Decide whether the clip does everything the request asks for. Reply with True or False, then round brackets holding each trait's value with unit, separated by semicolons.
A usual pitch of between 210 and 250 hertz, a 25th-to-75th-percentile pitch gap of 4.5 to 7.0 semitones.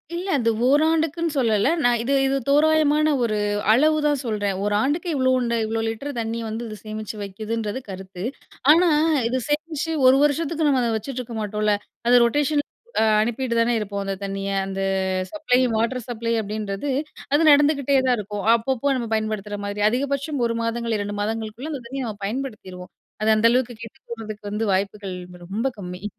True (230 Hz; 4.8 semitones)